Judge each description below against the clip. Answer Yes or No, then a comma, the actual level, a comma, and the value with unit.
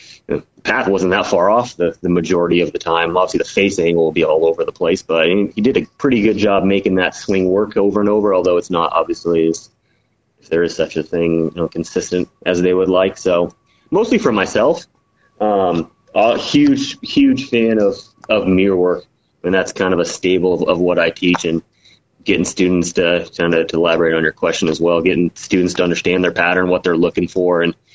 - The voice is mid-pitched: No, very low, 90 Hz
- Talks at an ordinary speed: No, fast, 225 wpm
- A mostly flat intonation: No, average, 3.8 semitones